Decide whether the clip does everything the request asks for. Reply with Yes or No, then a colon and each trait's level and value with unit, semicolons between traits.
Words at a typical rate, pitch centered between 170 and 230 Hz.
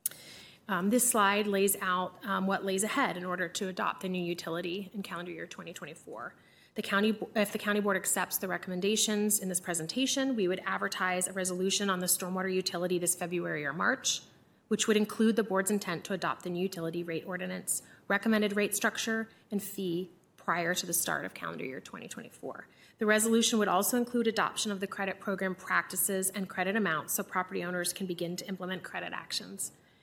Yes: average, 190 wpm; high, 190 Hz